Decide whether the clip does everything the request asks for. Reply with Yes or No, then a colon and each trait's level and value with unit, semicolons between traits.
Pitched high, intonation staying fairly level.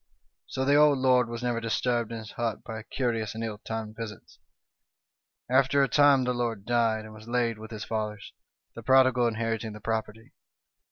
No: low, 115 Hz; narrow, 2.2 semitones